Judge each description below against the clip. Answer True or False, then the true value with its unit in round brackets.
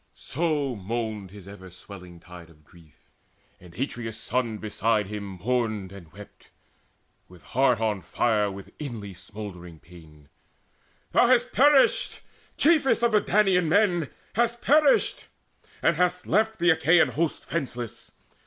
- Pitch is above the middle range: False (115 Hz)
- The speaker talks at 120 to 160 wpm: True (135 wpm)